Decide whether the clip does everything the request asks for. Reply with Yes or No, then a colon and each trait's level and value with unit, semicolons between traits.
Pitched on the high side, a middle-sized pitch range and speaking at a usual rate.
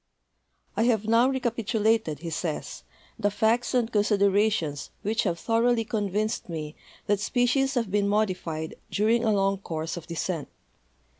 Yes: high, 210 Hz; average, 4.1 semitones; average, 145 wpm